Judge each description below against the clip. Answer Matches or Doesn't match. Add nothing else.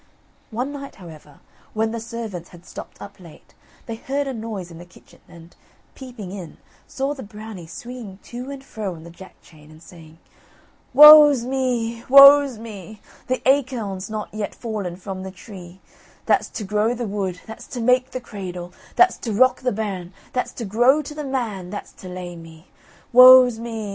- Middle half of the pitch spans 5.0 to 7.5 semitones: Matches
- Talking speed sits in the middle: Matches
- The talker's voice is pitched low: Doesn't match